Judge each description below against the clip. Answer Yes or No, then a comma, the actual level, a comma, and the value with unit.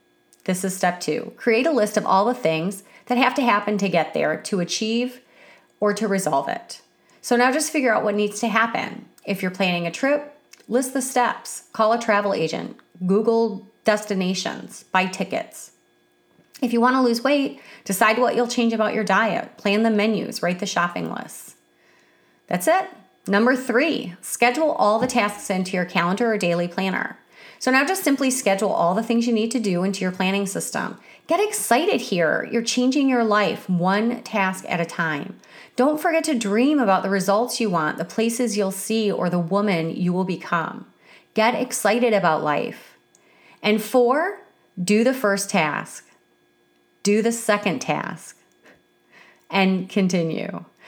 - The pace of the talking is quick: No, average, 170 wpm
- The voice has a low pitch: No, high, 215 Hz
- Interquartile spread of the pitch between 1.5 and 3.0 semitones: No, average, 4.3 semitones